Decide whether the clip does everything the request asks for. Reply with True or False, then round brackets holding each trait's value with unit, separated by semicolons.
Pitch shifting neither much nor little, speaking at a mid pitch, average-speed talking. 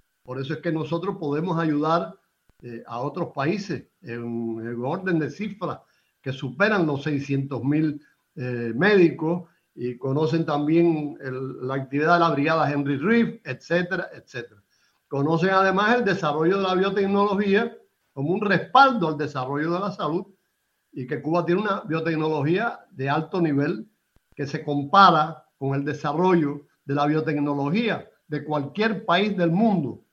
True (4.3 semitones; 155 Hz; 145 wpm)